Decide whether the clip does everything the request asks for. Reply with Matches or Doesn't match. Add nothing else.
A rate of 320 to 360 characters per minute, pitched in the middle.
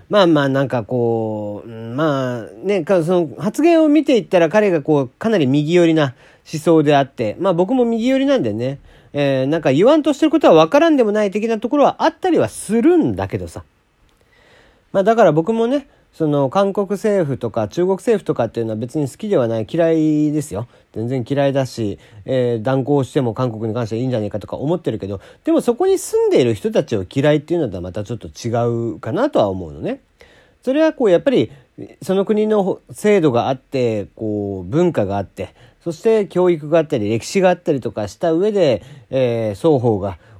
Doesn't match